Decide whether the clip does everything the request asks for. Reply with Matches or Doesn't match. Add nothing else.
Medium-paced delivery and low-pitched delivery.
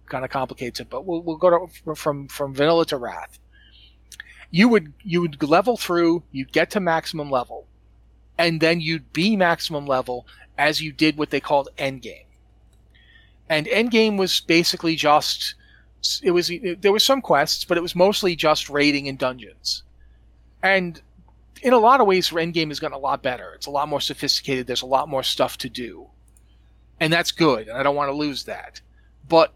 Doesn't match